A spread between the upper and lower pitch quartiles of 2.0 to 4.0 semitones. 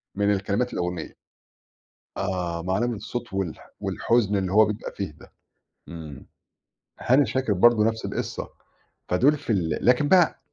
No: average, 4.9 semitones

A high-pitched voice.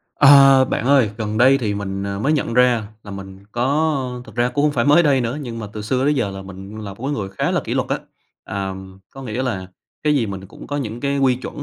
No: low, 120 Hz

